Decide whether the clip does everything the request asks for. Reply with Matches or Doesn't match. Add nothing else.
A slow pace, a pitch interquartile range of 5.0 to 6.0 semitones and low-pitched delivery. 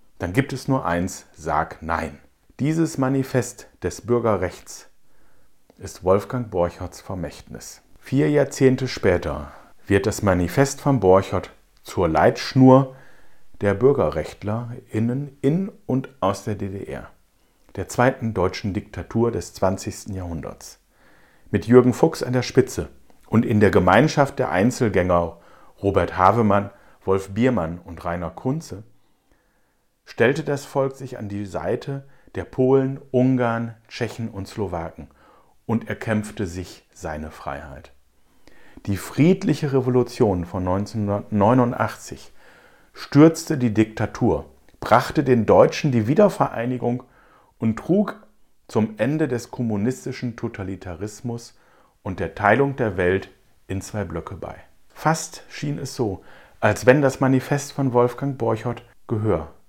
Matches